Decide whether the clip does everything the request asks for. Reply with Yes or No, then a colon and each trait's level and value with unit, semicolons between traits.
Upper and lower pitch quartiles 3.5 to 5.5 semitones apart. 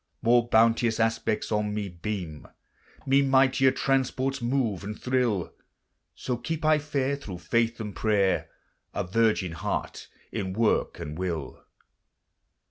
Yes: average, 4.8 semitones